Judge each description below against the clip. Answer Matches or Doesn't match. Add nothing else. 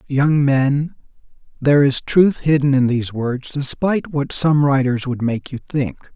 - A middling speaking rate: Matches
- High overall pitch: Doesn't match